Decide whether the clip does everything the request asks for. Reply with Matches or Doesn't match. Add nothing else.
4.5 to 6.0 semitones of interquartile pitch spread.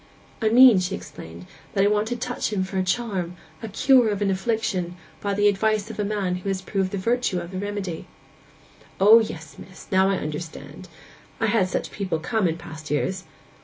Doesn't match